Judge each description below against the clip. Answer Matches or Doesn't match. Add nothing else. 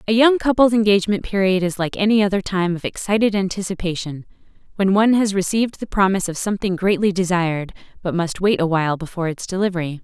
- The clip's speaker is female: Matches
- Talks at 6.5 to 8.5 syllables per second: Matches